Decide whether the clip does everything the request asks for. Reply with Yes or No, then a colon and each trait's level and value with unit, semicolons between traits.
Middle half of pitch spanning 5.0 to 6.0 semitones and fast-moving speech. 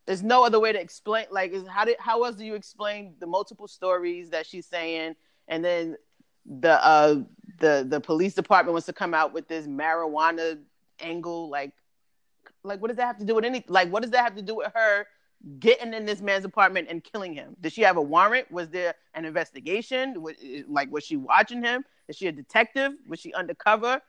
Yes: wide, 5.6 semitones; fast, 215 wpm